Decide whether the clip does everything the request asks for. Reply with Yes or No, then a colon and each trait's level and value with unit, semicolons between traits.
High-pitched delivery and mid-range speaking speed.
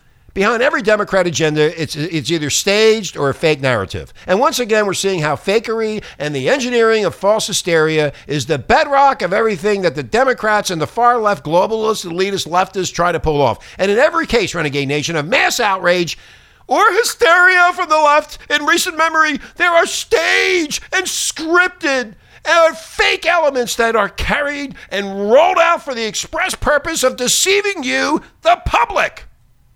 Yes: high, 220 Hz; average, 165 wpm